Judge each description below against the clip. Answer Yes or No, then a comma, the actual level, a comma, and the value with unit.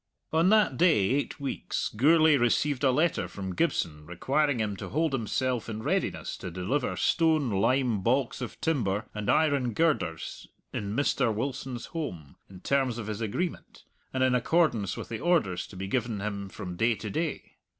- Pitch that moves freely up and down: Yes, wide, 6.0 semitones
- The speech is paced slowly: No, average, 170 wpm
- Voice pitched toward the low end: Yes, low, 125 Hz